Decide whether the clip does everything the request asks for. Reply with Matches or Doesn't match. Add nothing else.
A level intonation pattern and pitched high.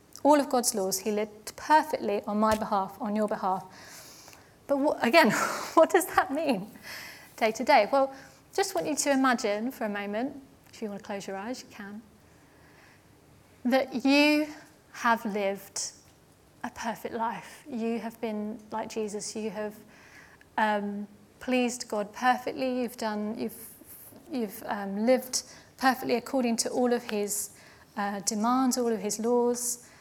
Doesn't match